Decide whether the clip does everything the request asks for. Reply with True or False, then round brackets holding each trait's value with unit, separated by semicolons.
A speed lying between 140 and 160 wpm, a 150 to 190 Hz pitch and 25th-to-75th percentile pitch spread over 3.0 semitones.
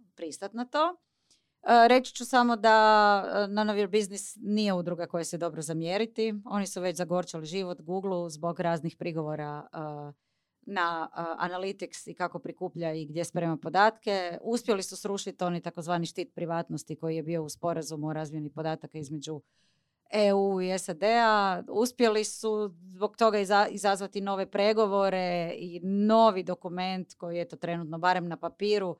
True (145 wpm; 185 Hz; 3.5 semitones)